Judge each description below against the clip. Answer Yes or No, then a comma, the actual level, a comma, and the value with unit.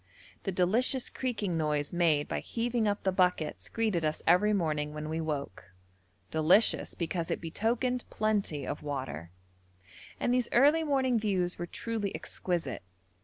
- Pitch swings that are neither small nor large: No, wide, 6.5 semitones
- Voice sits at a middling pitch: Yes, medium, 180 Hz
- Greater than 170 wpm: No, average, 145 wpm